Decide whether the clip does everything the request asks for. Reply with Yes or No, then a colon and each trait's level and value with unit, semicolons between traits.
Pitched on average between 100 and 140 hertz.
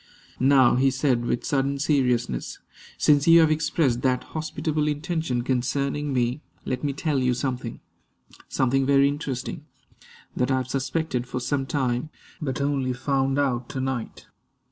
Yes: low, 135 Hz